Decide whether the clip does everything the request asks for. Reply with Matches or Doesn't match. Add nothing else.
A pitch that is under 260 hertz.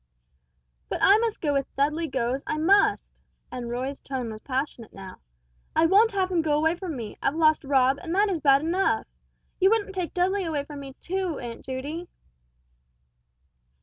Doesn't match